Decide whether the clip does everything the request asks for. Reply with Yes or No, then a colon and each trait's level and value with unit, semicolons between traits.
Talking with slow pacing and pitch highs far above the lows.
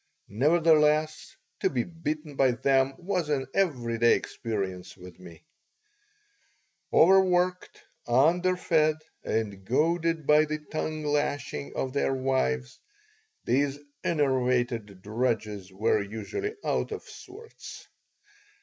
Yes: slow, 105 wpm; wide, 5.9 semitones